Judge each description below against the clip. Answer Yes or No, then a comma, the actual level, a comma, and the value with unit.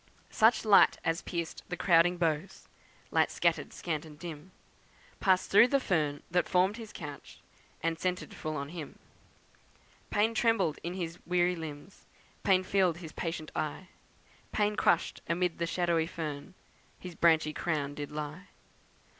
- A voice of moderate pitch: Yes, medium, 170 Hz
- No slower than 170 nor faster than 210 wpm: No, average, 145 wpm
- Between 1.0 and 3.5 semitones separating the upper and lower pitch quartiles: Yes, average, 3.0 semitones